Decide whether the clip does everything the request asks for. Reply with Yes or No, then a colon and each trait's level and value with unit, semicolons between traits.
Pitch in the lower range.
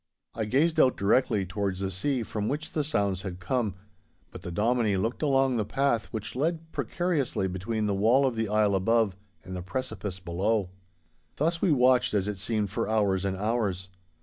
Yes: low, 110 Hz